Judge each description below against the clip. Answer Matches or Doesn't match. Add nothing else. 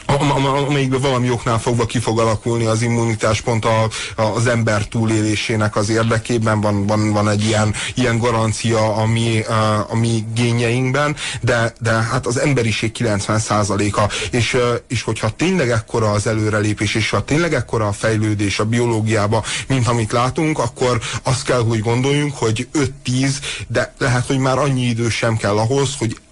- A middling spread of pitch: Doesn't match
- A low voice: Matches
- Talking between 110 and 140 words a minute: Doesn't match